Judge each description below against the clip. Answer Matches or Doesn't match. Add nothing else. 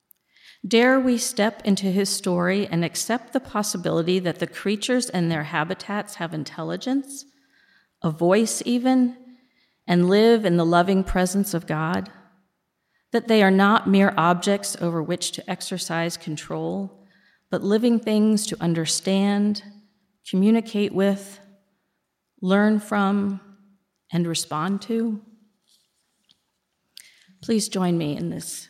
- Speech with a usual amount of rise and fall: Matches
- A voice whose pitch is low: Doesn't match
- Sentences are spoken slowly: Matches